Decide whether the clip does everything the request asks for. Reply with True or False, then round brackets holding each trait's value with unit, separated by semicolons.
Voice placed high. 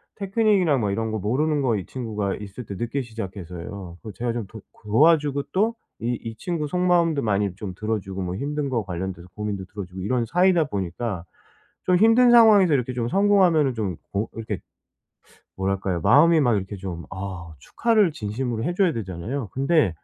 False (115 Hz)